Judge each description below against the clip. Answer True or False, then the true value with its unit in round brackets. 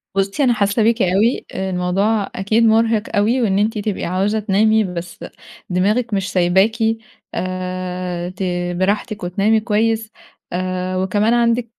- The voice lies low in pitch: False (200 Hz)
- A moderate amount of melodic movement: True (3.2 semitones)